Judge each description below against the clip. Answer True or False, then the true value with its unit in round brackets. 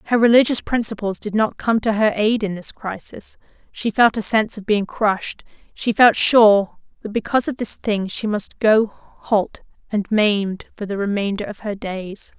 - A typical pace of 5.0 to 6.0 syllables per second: False (4.7 syllables/s)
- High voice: True (210 Hz)